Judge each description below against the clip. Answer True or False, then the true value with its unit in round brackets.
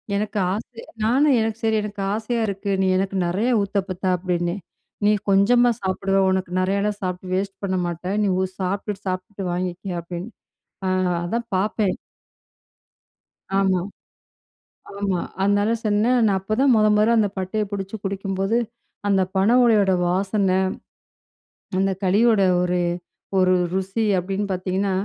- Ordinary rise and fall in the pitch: False (2.2 semitones)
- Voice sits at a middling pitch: False (195 Hz)